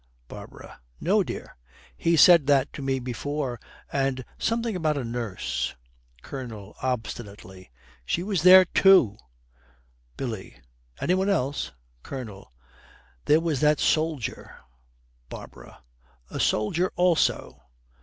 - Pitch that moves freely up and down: Yes, wide, 6.6 semitones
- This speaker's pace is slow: Yes, slow, 110 wpm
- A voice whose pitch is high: No, low, 135 Hz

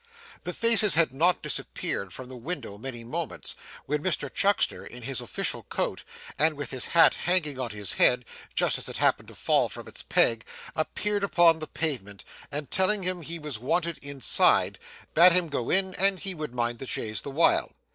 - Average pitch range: No, wide, 6.1 semitones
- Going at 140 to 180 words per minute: No, average, 190 wpm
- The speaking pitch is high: No, medium, 150 Hz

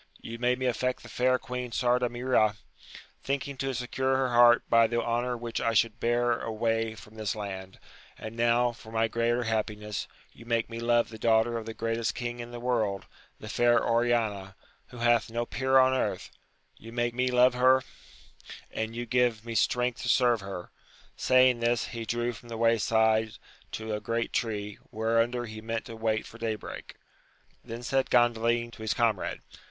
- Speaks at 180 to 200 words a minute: Yes, average, 185 wpm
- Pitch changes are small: Yes, narrow, 1.6 semitones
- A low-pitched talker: Yes, low, 115 Hz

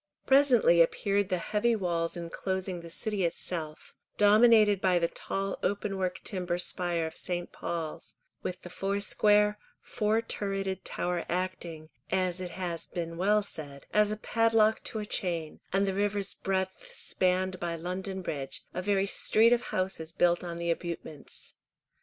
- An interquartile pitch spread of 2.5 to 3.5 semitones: Yes, average, 3.0 semitones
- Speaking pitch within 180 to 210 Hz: Yes, medium, 185 Hz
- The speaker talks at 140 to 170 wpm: Yes, average, 150 wpm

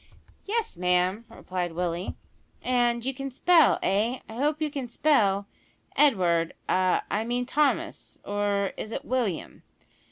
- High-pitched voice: Yes, high, 225 Hz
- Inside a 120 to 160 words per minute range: Yes, slow, 135 wpm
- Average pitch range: No, wide, 6.4 semitones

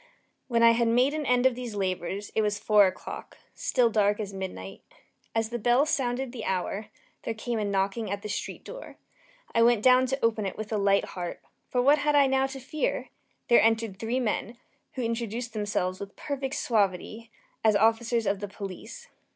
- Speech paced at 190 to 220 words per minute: Yes, average, 195 wpm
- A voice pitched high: Yes, high, 225 Hz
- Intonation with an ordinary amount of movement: Yes, average, 3.5 semitones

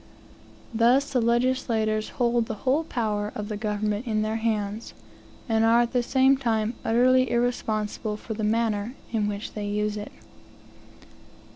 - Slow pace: No, average, 150 wpm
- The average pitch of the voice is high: Yes, high, 225 Hz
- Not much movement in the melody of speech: Yes, narrow, 2.2 semitones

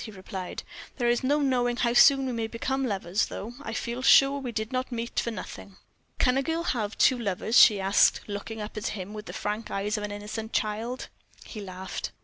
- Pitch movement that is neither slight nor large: Yes, average, 3.4 semitones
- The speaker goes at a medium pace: No, fast, 215 wpm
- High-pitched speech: Yes, high, 225 Hz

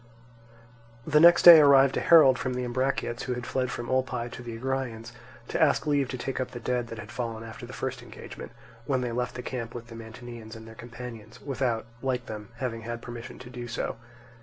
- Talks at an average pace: No, fast, 215 wpm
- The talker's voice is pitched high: No, low, 120 Hz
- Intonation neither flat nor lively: No, narrow, 2.1 semitones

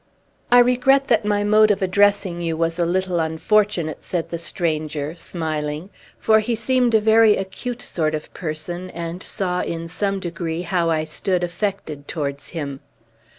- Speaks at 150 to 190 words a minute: Yes, average, 160 wpm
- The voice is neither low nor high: Yes, medium, 175 Hz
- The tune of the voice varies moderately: Yes, average, 4.2 semitones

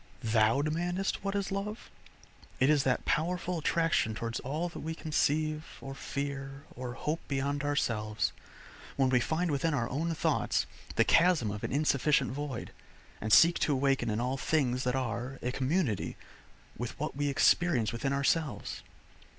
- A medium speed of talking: Yes, average, 160 wpm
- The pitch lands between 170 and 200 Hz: No, medium, 140 Hz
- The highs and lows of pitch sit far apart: No, average, 4.1 semitones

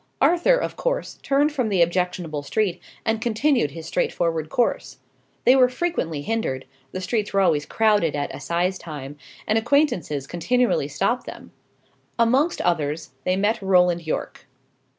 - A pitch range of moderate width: No, wide, 6.9 semitones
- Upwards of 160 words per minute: No, average, 145 wpm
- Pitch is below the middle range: No, high, 190 Hz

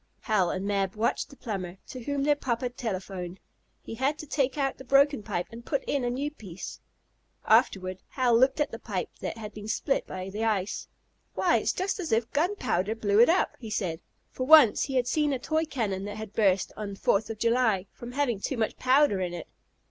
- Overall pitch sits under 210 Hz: No, high, 230 Hz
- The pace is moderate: No, fast, 215 wpm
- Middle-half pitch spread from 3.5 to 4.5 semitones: No, wide, 5.5 semitones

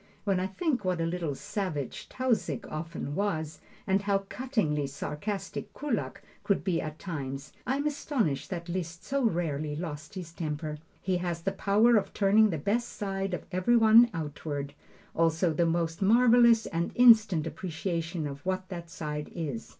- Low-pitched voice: No, medium, 175 Hz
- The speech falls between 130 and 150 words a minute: No, average, 165 wpm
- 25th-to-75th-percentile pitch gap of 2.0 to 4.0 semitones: No, average, 4.7 semitones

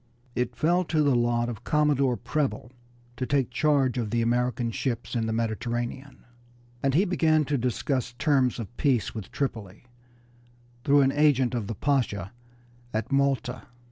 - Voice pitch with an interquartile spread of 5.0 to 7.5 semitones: No, average, 3.2 semitones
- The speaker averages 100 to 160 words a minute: Yes, average, 155 wpm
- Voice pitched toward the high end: No, low, 125 Hz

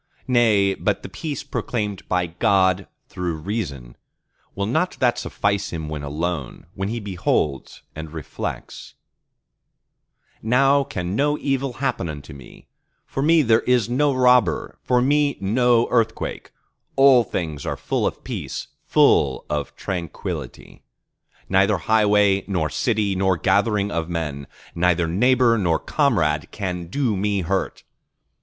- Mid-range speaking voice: No, low, 100 Hz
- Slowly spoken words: Yes, slow, 130 wpm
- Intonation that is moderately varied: No, wide, 6.1 semitones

